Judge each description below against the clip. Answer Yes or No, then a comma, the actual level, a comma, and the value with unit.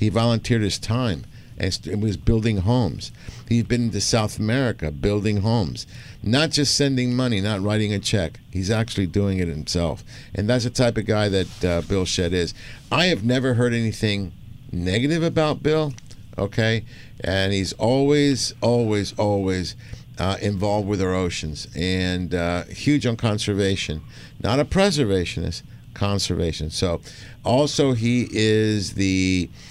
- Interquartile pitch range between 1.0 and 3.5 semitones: No, average, 4.1 semitones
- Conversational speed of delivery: Yes, average, 145 wpm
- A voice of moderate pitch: No, low, 110 Hz